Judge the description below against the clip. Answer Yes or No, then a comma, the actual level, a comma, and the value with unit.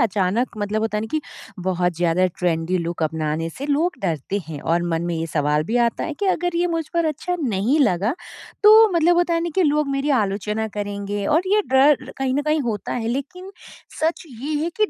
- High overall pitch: Yes, high, 230 Hz